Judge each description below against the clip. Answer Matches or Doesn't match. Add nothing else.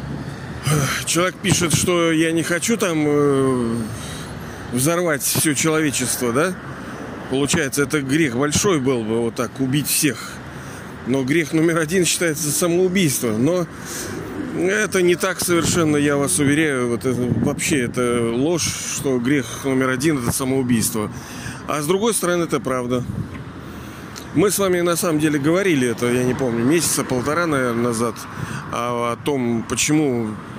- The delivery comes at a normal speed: Matches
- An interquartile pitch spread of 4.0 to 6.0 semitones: Matches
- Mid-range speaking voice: Matches